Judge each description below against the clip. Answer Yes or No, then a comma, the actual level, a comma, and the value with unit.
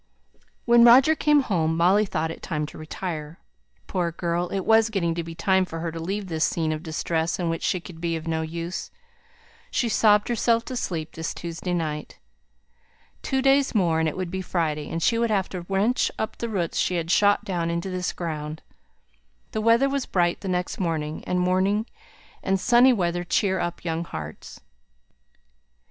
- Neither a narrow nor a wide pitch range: Yes, average, 4.0 semitones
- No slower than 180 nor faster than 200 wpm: Yes, average, 190 wpm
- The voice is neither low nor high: Yes, medium, 180 Hz